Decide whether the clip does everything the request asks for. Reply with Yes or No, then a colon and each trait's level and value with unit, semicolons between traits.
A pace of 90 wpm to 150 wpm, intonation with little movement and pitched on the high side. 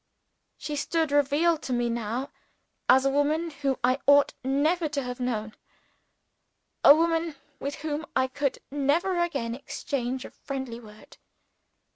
No: average, 140 wpm; average, 3.4 semitones; very high, 280 Hz